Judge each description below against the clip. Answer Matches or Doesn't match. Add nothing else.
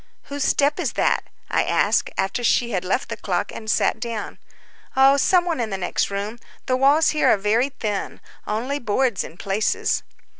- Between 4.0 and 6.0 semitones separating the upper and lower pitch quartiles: Matches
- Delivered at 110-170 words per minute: Doesn't match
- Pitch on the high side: Matches